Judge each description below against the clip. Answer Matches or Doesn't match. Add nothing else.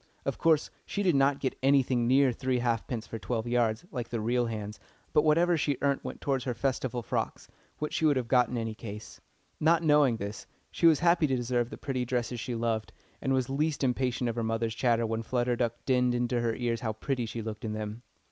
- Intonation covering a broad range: Doesn't match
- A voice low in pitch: Matches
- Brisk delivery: Matches